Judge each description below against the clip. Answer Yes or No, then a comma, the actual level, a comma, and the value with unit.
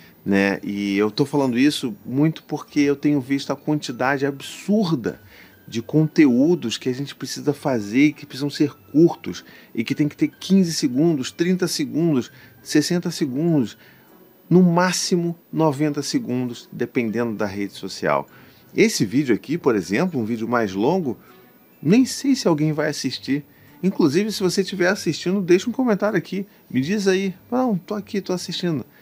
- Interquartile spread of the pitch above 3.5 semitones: Yes, average, 5.2 semitones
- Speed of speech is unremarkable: Yes, average, 160 wpm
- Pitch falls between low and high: Yes, medium, 150 Hz